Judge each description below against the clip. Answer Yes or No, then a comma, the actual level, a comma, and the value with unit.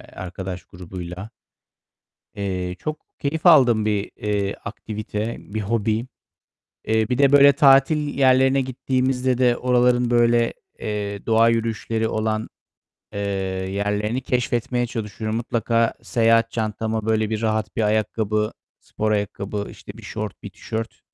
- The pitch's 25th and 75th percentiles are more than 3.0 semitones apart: No, narrow, 2.6 semitones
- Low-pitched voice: Yes, low, 110 Hz